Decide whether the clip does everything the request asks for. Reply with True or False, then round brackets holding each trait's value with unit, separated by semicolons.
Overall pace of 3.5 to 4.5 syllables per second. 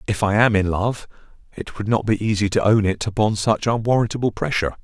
False (6.0 syllables/s)